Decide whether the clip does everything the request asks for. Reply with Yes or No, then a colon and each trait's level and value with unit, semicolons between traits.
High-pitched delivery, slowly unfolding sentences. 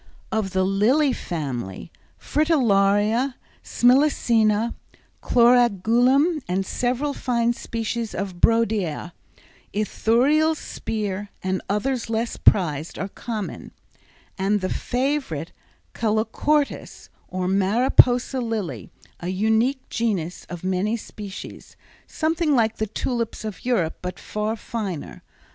Yes: high, 220 Hz; slow, 100 wpm